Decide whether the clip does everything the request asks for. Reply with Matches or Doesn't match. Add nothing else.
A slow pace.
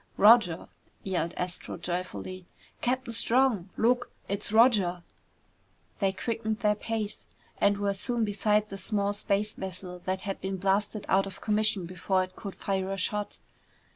Doesn't match